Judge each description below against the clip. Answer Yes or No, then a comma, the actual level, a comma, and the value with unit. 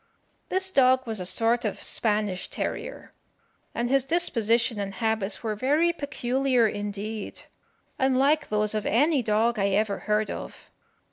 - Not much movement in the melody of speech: No, average, 4.0 semitones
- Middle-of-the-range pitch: No, high, 230 Hz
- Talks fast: No, average, 140 wpm